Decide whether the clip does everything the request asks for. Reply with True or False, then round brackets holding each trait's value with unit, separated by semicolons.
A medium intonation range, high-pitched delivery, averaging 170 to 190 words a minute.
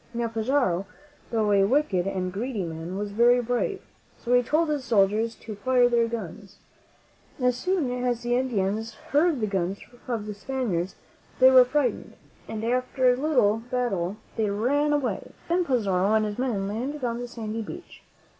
True (3.8 semitones; 235 Hz; 175 wpm)